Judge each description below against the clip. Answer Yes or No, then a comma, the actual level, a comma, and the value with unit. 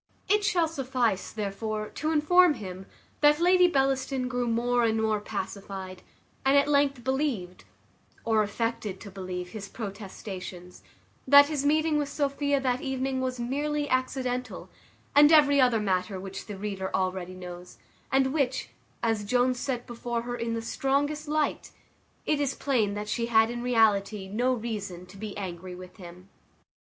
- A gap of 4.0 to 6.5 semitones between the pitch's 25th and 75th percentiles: Yes, wide, 5.5 semitones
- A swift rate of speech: No, average, 155 wpm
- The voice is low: No, high, 240 Hz